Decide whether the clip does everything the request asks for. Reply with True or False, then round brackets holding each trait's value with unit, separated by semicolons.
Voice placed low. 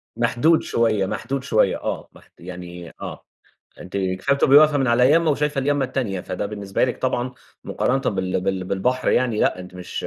True (120 Hz)